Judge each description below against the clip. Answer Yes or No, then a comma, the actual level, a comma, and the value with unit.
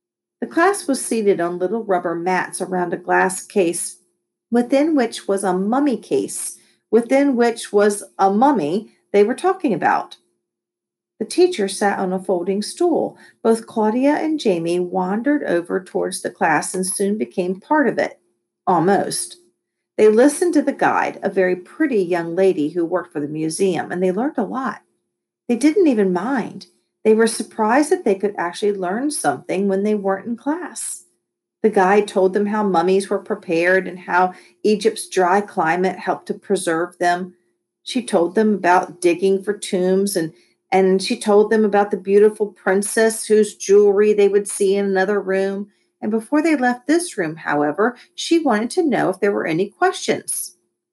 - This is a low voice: No, high, 205 Hz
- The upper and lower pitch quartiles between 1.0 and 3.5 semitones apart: No, average, 4.3 semitones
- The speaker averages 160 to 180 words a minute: Yes, average, 170 wpm